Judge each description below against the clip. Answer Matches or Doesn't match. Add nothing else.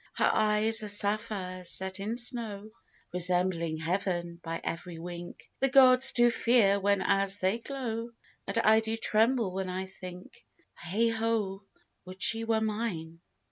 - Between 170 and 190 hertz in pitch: Doesn't match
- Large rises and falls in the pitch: Doesn't match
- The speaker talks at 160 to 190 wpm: Doesn't match